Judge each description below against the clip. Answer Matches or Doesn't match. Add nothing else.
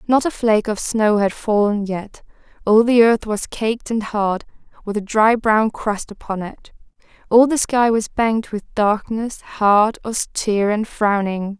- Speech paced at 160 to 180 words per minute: Matches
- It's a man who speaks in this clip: Doesn't match